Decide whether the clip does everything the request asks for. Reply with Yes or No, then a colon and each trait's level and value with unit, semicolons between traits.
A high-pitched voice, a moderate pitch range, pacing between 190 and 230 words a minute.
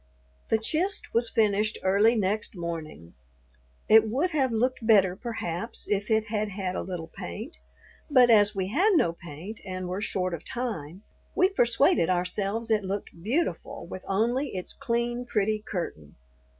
No: high, 210 Hz; average, 4.3 semitones; average, 155 wpm